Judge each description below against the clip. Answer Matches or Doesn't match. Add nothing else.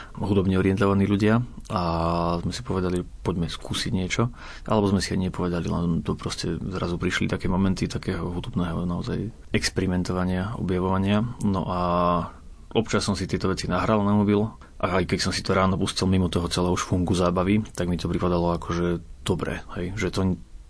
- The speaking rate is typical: Doesn't match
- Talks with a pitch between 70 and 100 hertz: Matches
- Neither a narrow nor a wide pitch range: Doesn't match